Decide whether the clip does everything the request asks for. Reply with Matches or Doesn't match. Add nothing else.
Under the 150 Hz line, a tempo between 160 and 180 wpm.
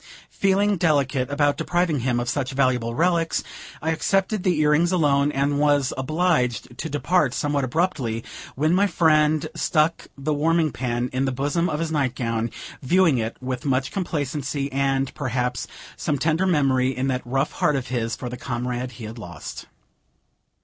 Matches